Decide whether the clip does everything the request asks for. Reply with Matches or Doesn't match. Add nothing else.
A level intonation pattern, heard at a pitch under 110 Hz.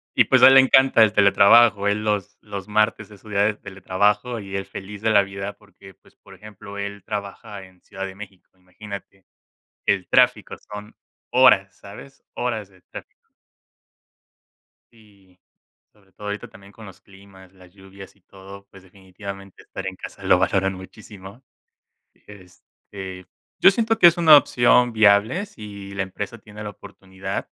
Matches